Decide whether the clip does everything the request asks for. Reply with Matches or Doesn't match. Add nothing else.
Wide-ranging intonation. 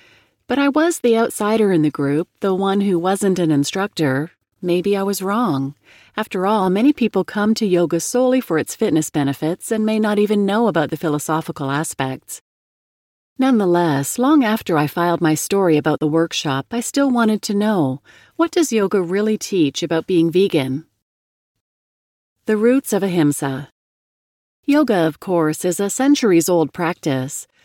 Matches